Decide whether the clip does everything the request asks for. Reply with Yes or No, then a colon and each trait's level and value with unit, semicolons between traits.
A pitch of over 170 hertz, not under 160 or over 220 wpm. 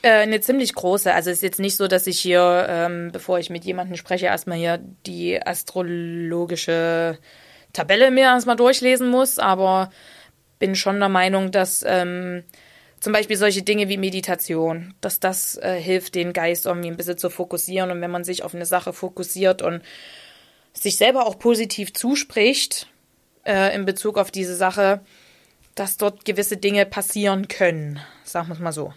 Yes: medium, 185 Hz; average, 170 wpm